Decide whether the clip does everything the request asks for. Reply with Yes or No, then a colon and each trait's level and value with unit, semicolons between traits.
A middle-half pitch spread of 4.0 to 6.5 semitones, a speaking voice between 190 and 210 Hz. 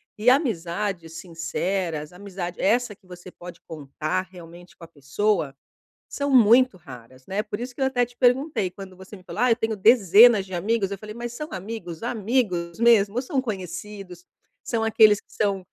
Yes: average, 4.6 semitones; high, 200 Hz